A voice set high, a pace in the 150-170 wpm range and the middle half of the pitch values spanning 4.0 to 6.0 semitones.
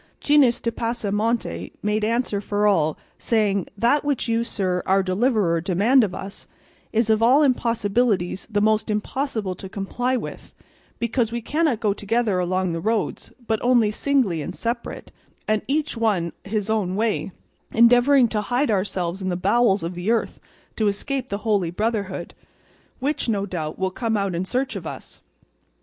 No: high, 215 Hz; average, 165 wpm; average, 3.6 semitones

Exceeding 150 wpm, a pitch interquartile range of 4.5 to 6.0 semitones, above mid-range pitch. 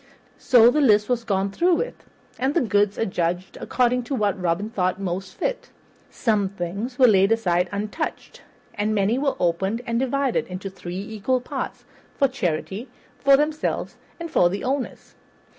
Yes: average, 160 wpm; average, 5.1 semitones; high, 215 Hz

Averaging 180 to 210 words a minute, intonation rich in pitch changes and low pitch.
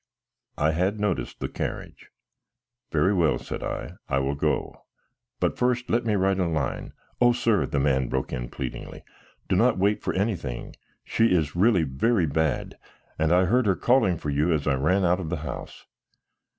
Yes: average, 185 wpm; wide, 6.0 semitones; very low, 90 Hz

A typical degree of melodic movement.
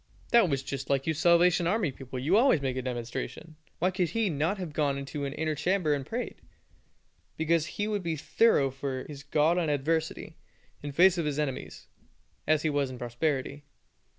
Yes: average, 3.8 semitones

